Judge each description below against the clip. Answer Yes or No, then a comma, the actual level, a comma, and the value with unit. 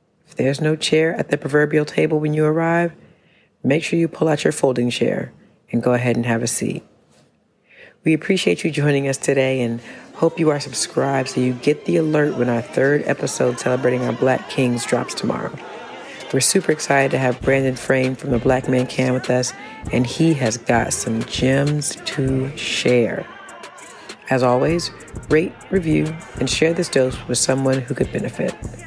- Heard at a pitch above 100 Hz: Yes, low, 135 Hz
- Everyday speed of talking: Yes, average, 180 wpm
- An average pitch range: Yes, average, 3.5 semitones